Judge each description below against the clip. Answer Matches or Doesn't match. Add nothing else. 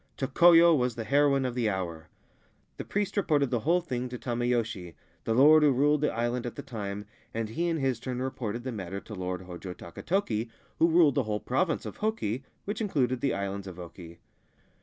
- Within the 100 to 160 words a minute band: Doesn't match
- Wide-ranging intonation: Matches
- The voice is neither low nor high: Doesn't match